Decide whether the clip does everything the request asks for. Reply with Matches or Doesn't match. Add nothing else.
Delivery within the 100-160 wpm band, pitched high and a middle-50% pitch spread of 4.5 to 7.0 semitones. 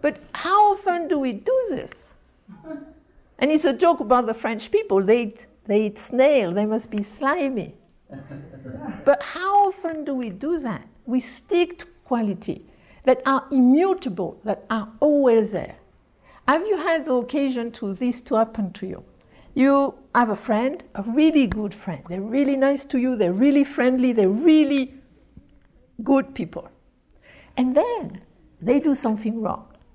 Matches